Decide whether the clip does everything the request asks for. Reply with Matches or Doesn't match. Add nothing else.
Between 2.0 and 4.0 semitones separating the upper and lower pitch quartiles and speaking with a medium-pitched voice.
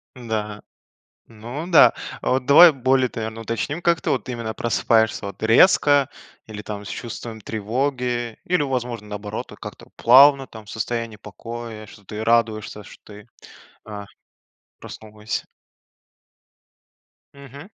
Doesn't match